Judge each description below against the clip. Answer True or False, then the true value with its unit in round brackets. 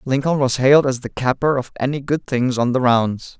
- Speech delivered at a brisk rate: True (230 wpm)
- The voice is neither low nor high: False (130 Hz)